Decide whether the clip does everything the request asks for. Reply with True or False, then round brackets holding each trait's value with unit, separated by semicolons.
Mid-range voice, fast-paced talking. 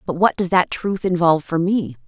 True (175 Hz; 230 wpm)